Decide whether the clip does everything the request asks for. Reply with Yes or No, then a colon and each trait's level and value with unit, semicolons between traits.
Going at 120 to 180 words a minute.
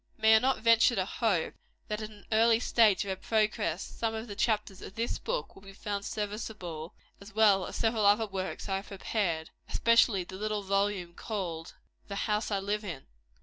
No: average, 195 wpm